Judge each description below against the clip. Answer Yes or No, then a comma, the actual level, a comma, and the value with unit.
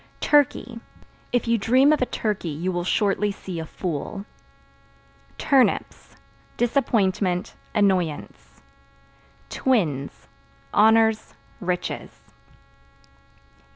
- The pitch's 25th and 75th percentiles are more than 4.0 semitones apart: Yes, average, 4.6 semitones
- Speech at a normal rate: No, slow, 85 wpm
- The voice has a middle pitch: No, high, 205 Hz